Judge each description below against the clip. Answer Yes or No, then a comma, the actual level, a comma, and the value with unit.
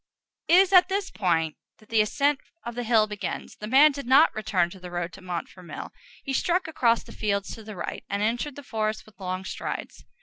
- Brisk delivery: Yes, fast, 215 wpm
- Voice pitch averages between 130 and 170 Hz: No, high, 215 Hz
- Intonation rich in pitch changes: Yes, wide, 6.5 semitones